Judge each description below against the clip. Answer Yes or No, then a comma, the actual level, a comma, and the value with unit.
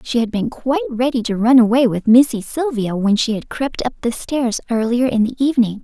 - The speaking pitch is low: No, high, 240 Hz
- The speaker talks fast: Yes, fast, 225 wpm